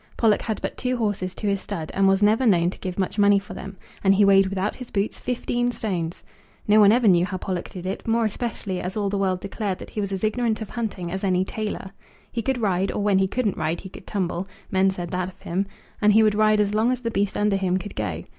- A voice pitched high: Yes, high, 200 Hz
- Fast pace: Yes, fast, 260 wpm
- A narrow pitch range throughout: Yes, narrow, 2.3 semitones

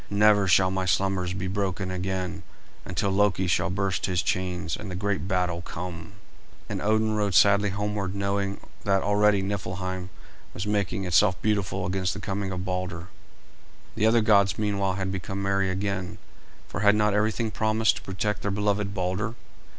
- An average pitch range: No, narrow, 1.8 semitones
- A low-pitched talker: Yes, very low, 95 Hz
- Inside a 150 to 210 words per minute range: Yes, average, 165 wpm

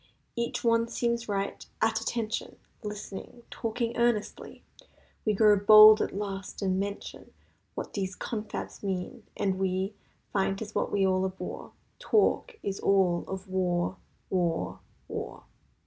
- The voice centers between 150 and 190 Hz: No, high, 200 Hz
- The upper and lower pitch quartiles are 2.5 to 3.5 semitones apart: Yes, average, 2.8 semitones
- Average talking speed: No, slow, 115 wpm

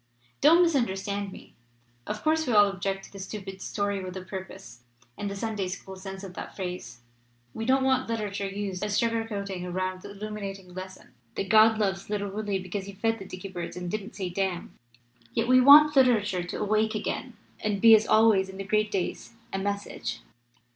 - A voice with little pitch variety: Yes, narrow, 2.3 semitones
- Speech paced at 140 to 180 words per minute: No, average, 200 wpm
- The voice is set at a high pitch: Yes, high, 200 Hz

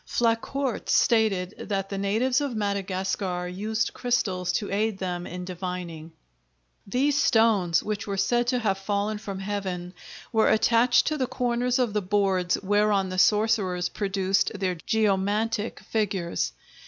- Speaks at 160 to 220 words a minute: No, average, 140 wpm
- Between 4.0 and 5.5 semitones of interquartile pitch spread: No, average, 3.0 semitones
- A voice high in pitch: Yes, high, 205 Hz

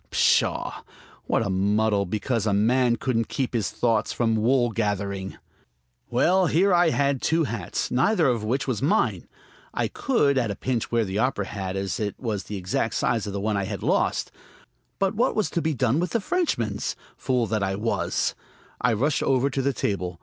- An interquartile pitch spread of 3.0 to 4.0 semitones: No, average, 5.2 semitones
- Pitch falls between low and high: No, low, 115 Hz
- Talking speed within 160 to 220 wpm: Yes, average, 195 wpm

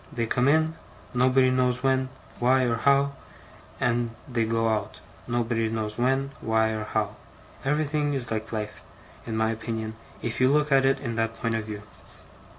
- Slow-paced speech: No, average, 170 wpm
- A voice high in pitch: No, low, 120 Hz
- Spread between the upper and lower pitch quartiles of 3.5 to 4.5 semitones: No, average, 3.0 semitones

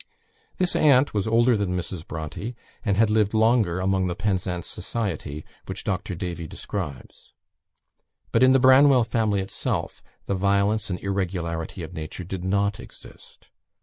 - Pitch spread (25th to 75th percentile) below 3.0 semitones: No, average, 3.8 semitones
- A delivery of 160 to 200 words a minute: No, average, 150 wpm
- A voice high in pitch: No, low, 100 Hz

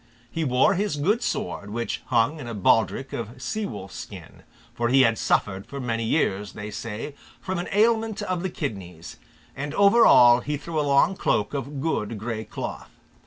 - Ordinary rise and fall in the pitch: No, wide, 6.7 semitones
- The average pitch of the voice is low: Yes, low, 130 Hz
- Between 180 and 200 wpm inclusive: Yes, average, 185 wpm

